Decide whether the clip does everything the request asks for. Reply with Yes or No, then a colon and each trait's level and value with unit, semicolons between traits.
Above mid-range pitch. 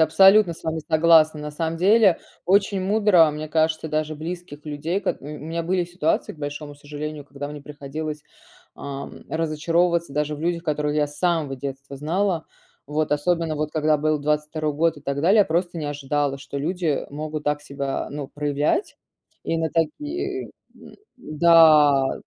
No: medium, 155 Hz